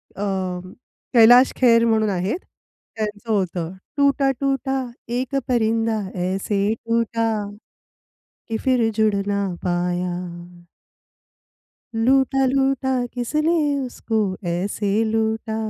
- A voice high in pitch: Yes, high, 225 Hz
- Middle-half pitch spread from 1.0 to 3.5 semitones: No, average, 4.2 semitones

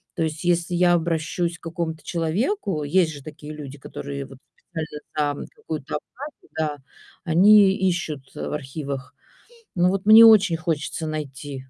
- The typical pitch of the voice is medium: Yes, medium, 160 Hz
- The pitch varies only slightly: No, average, 3.1 semitones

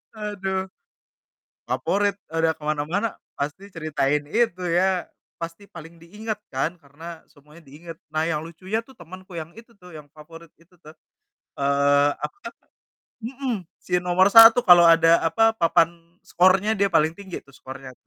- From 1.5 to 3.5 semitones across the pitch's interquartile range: No, average, 3.9 semitones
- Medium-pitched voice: Yes, medium, 170 Hz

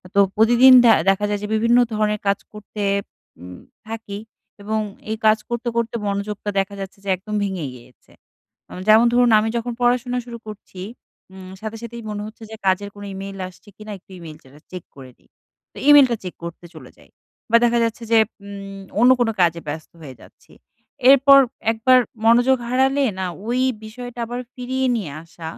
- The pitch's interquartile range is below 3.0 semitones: No, average, 3.6 semitones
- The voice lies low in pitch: No, high, 215 Hz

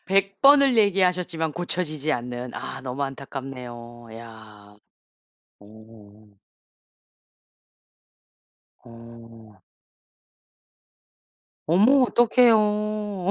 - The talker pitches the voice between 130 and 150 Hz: Yes, medium, 140 Hz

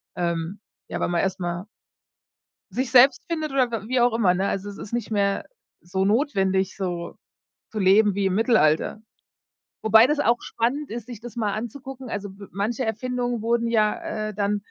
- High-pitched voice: Yes, high, 215 Hz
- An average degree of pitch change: Yes, average, 3.5 semitones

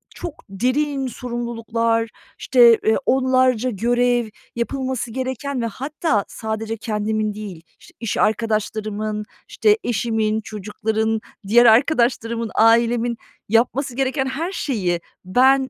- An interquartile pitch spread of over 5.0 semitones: No, average, 2.9 semitones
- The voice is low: No, high, 235 Hz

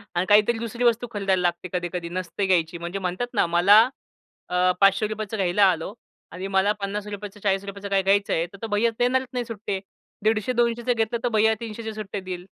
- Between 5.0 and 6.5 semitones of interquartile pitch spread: No, average, 3.0 semitones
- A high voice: Yes, high, 205 Hz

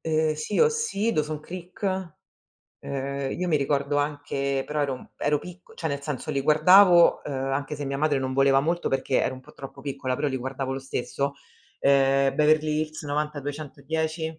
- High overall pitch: No, medium, 145 Hz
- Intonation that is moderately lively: No, narrow, 2.3 semitones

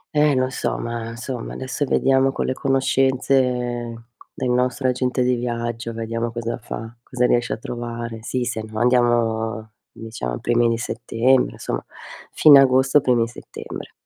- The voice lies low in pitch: Yes, low, 120 Hz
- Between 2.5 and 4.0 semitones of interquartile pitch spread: No, narrow, 1.9 semitones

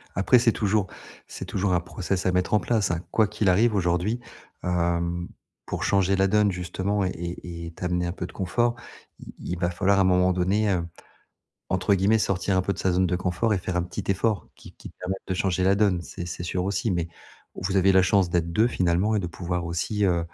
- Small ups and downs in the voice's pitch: Yes, narrow, 2.2 semitones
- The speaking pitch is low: Yes, very low, 95 Hz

